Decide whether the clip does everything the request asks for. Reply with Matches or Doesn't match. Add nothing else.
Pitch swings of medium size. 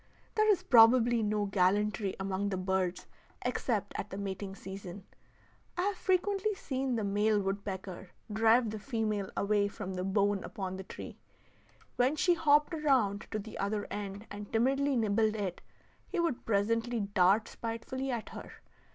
Matches